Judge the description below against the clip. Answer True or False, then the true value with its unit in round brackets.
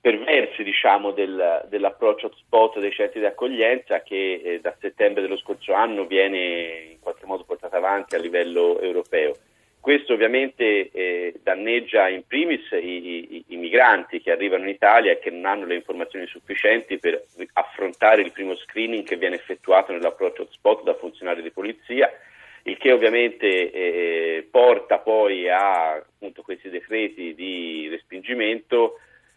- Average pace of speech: True (145 wpm)